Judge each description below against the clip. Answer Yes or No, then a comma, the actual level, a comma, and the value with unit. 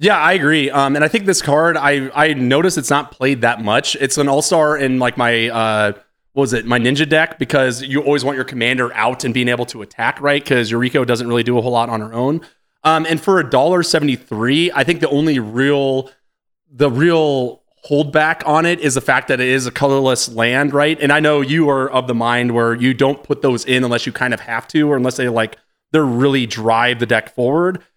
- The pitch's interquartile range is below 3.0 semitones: No, average, 3.4 semitones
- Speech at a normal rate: No, fast, 230 wpm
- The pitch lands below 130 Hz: No, low, 135 Hz